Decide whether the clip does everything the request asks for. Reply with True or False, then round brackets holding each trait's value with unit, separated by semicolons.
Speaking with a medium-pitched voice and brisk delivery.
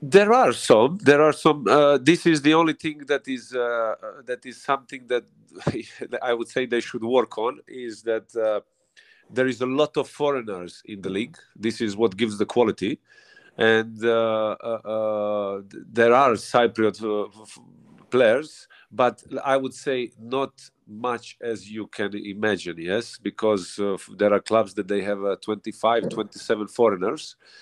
False (115 Hz; 175 wpm)